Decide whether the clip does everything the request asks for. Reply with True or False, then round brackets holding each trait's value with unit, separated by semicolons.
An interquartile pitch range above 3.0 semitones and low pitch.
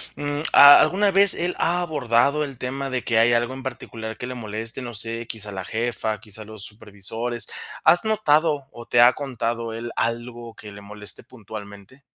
True (3.9 semitones; 120 Hz)